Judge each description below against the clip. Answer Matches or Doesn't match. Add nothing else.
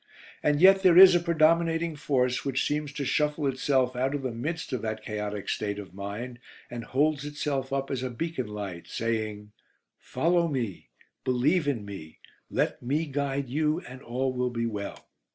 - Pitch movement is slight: Doesn't match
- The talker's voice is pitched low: Matches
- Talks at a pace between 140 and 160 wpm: Doesn't match